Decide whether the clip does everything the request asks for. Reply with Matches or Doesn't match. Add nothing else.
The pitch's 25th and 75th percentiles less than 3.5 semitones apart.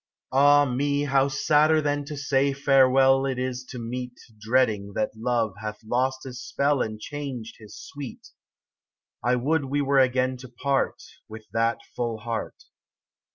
Matches